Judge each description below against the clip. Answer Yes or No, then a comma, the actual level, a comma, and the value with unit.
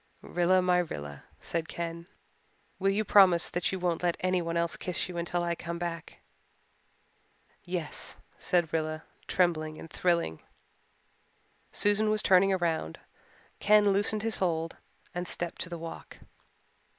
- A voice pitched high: No, medium, 175 Hz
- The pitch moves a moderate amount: No, narrow, 1.8 semitones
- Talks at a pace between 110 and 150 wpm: Yes, average, 140 wpm